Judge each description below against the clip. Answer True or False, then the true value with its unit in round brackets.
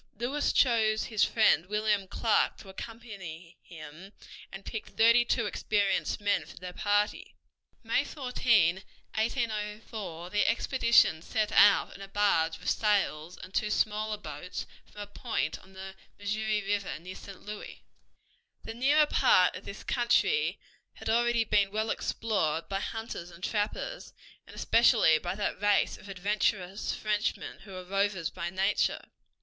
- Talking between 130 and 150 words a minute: True (145 wpm)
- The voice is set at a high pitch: True (205 Hz)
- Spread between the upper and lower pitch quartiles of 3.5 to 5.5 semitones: False (2.9 semitones)